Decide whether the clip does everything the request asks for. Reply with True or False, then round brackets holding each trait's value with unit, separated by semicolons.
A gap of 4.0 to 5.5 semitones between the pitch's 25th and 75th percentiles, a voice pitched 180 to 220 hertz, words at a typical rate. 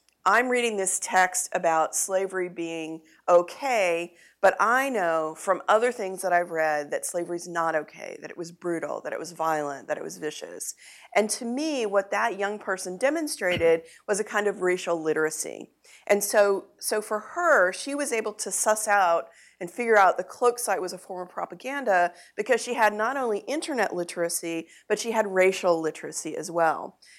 True (4.4 semitones; 190 Hz; 185 wpm)